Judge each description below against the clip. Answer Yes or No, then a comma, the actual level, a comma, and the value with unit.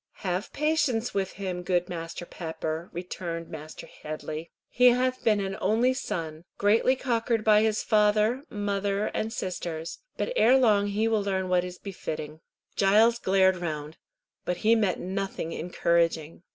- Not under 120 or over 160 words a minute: Yes, average, 145 wpm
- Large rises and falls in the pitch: No, average, 4.3 semitones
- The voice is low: No, high, 195 Hz